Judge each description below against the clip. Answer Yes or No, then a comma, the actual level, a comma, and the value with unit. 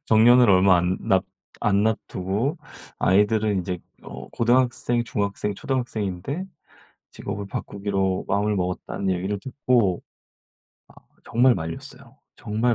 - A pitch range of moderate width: Yes, average, 3.9 semitones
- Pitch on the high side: No, low, 105 Hz